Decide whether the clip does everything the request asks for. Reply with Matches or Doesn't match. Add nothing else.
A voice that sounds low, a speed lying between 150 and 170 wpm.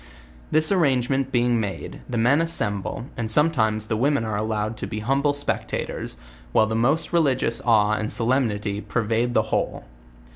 Matches